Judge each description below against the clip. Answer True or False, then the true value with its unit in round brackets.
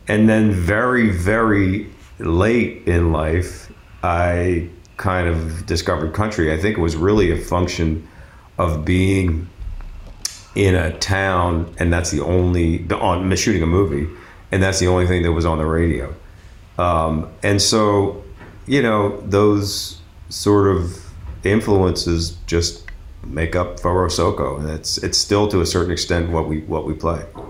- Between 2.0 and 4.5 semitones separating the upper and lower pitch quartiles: True (2.9 semitones)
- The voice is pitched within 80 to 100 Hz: True (90 Hz)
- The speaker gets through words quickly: False (150 wpm)